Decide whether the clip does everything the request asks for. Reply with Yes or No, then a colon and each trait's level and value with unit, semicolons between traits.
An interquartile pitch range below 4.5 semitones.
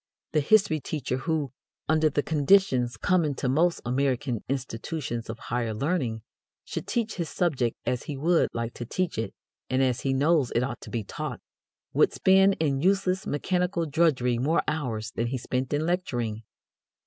No: average, 5.3 semitones